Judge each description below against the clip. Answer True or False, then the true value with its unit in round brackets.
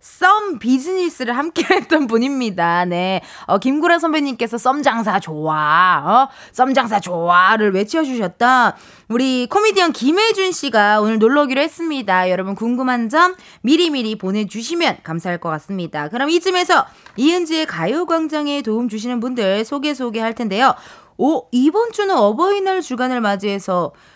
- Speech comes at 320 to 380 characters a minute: True (330 characters per minute)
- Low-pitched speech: False (255 Hz)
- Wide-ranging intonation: True (7.5 semitones)